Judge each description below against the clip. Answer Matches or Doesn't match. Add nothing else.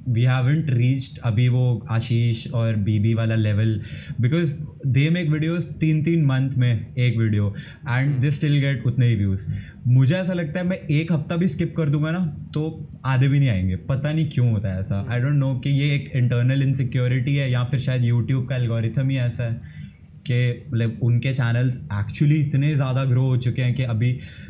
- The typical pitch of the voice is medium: Doesn't match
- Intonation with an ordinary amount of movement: Matches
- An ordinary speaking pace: Doesn't match